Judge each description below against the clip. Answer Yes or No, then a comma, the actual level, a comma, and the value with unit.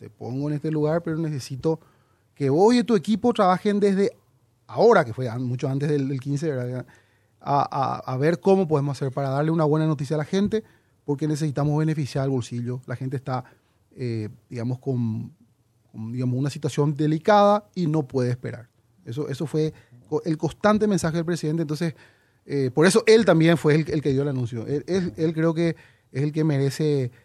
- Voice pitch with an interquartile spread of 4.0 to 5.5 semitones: Yes, average, 4.4 semitones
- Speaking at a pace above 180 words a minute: Yes, fast, 190 wpm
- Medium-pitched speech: Yes, medium, 145 Hz